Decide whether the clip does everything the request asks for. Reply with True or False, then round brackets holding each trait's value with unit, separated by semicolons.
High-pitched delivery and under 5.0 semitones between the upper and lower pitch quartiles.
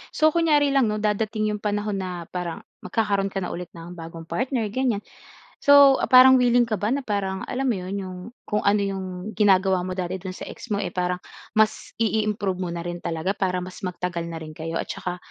True (200 Hz; 3.5 semitones)